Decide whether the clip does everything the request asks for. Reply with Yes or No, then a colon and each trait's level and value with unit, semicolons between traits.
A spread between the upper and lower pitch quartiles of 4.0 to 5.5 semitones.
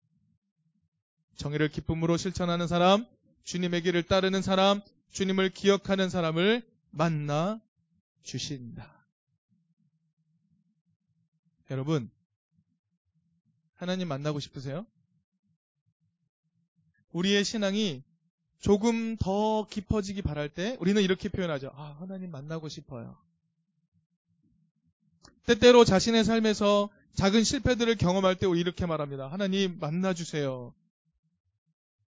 No: average, 3.6 semitones